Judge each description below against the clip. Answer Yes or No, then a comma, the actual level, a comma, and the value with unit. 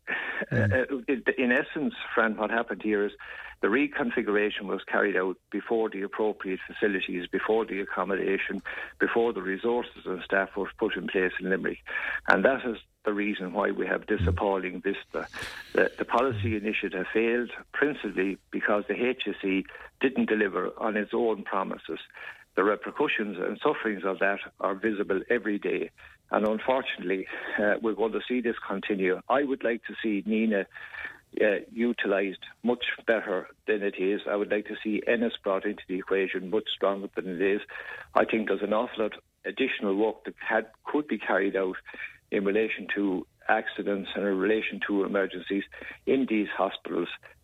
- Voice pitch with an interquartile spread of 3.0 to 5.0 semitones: No, narrow, 2.6 semitones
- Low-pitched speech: Yes, low, 105 Hz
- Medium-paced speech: Yes, average, 165 wpm